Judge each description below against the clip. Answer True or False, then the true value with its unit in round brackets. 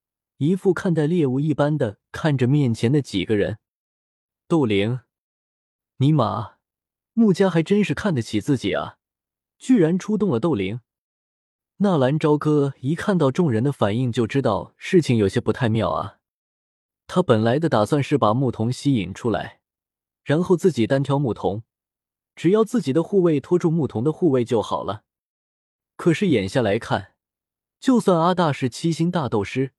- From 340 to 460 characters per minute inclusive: False (235 characters per minute)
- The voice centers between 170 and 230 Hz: False (140 Hz)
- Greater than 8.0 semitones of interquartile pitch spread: False (7.1 semitones)